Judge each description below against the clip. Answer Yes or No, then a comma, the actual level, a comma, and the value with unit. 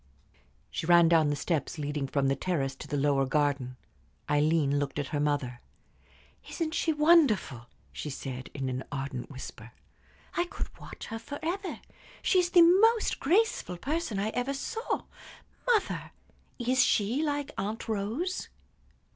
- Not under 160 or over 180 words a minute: No, average, 145 wpm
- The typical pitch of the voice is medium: Yes, medium, 175 Hz